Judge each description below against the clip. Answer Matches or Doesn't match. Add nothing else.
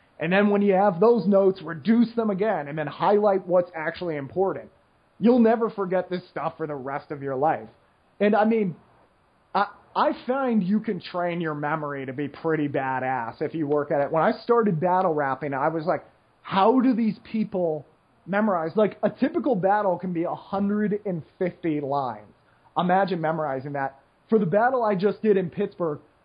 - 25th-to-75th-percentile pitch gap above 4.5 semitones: Matches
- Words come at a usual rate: Matches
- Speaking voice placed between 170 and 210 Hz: Matches